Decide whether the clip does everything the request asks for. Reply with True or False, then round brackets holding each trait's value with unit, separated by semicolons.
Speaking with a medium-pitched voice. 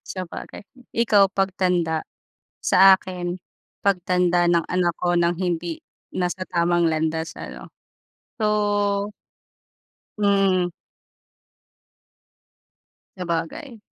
True (180 Hz)